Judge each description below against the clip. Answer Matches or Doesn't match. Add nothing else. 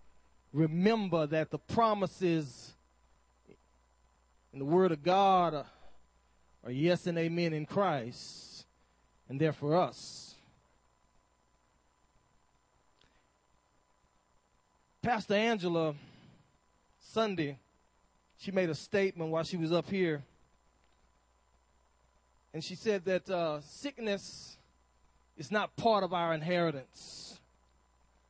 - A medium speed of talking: Doesn't match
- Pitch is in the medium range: Matches